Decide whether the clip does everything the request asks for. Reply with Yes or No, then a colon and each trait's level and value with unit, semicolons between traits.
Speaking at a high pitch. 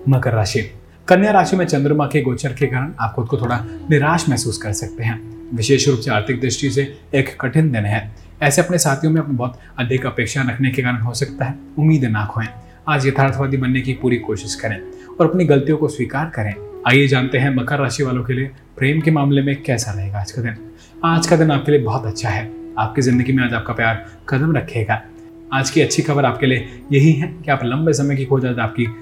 No: low, 135 Hz